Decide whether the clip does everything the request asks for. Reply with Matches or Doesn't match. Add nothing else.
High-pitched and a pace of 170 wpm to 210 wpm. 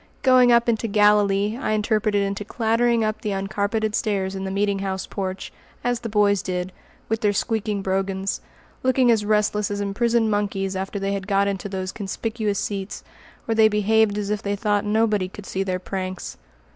Matches